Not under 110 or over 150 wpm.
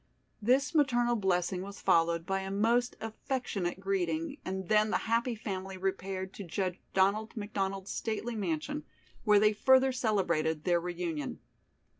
Yes: average, 140 wpm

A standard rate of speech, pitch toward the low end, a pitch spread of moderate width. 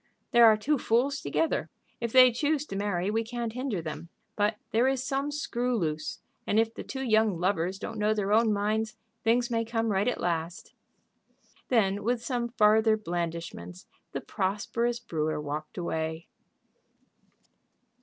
No: average, 155 wpm; high, 220 Hz; average, 4.7 semitones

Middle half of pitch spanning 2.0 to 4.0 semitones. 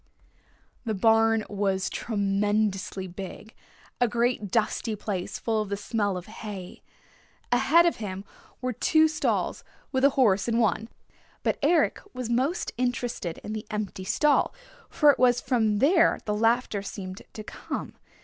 Yes: average, 3.4 semitones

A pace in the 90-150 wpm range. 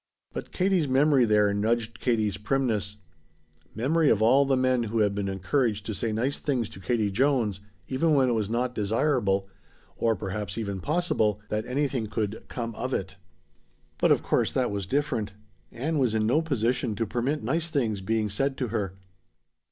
No: average, 175 wpm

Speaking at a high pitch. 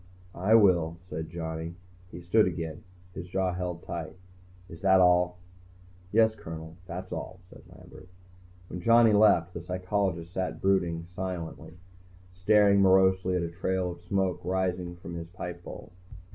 No: very low, 90 Hz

